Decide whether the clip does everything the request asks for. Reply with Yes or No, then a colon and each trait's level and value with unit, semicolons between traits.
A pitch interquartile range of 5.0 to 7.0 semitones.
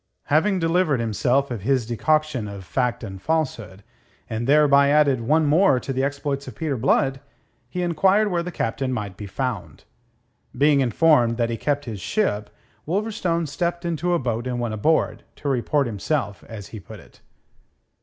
Yes: average, 5.3 semitones